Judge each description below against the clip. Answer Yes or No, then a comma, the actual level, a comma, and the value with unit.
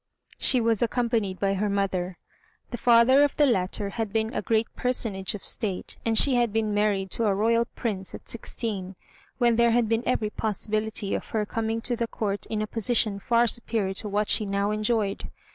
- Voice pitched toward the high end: Yes, high, 220 Hz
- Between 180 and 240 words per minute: Yes, average, 195 wpm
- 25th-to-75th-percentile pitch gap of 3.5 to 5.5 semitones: No, narrow, 2.6 semitones